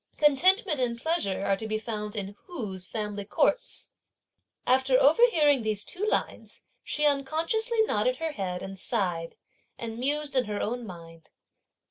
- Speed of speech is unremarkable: Yes, average, 145 wpm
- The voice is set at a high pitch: Yes, high, 245 Hz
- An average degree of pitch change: No, wide, 7.0 semitones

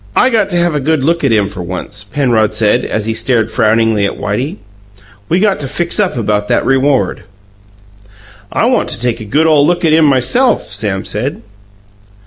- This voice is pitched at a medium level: No, low, 130 Hz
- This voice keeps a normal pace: Yes, average, 195 wpm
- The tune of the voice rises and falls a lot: Yes, wide, 6.9 semitones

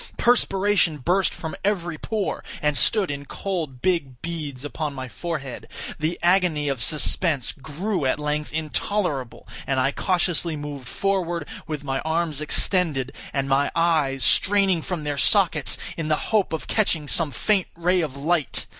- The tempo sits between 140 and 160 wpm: Yes, average, 155 wpm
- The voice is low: No, medium, 160 Hz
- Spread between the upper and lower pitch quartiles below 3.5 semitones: No, average, 4.1 semitones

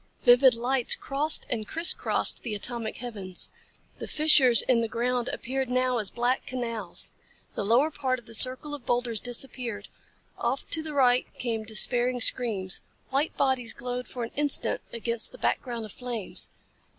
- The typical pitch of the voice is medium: No, high, 245 Hz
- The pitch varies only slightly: Yes, narrow, 2.1 semitones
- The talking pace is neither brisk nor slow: Yes, average, 165 wpm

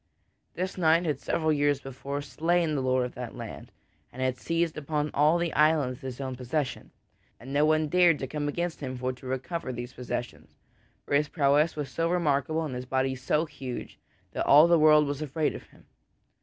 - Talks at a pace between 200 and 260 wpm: Yes, fast, 205 wpm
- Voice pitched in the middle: Yes, medium, 145 Hz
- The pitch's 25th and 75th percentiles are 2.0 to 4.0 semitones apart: Yes, average, 3.4 semitones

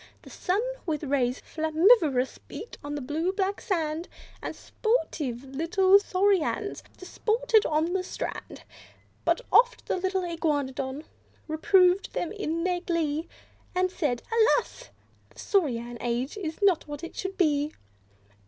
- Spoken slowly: Yes, slow, 130 wpm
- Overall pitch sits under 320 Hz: No, very high, 335 Hz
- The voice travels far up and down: No, average, 4.7 semitones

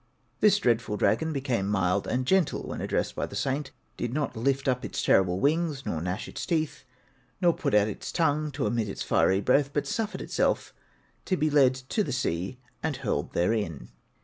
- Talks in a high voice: No, low, 130 Hz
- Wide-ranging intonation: Yes, wide, 6.5 semitones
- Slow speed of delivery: No, average, 190 wpm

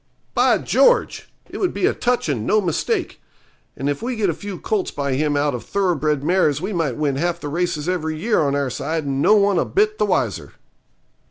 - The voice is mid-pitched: Yes, medium, 165 Hz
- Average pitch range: No, wide, 5.9 semitones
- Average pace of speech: No, fast, 225 wpm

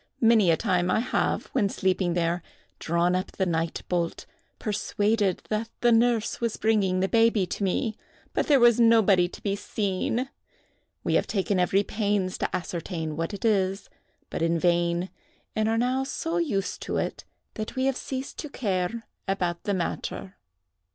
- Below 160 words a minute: No, average, 170 wpm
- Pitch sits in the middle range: No, high, 200 Hz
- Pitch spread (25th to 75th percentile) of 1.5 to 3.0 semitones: No, average, 4.1 semitones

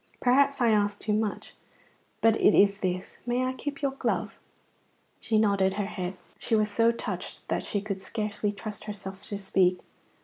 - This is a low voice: No, high, 210 Hz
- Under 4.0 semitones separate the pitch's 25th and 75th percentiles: Yes, narrow, 2.5 semitones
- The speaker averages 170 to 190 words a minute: Yes, average, 175 wpm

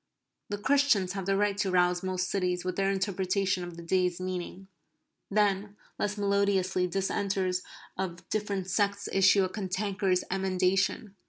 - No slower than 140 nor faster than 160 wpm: Yes, average, 145 wpm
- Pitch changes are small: Yes, narrow, 1.6 semitones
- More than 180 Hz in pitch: Yes, high, 190 Hz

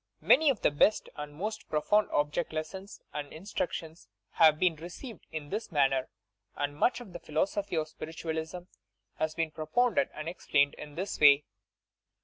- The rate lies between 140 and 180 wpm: Yes, average, 155 wpm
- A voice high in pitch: No, medium, 160 Hz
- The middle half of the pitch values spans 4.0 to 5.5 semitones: Yes, average, 4.4 semitones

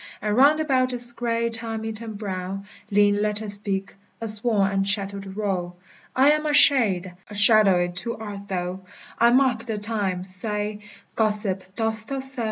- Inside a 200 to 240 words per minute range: No, average, 165 wpm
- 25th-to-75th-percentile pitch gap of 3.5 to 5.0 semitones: No, average, 3.0 semitones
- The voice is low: No, high, 210 Hz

